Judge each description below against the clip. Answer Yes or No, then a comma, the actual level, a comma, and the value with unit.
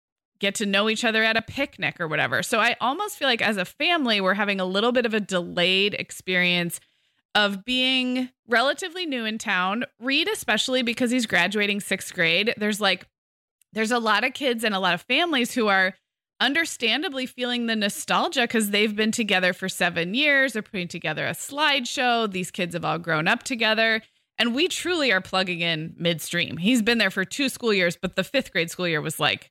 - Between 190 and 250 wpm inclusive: Yes, average, 200 wpm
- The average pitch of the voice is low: No, high, 215 Hz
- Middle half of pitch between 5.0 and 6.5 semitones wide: Yes, wide, 5.4 semitones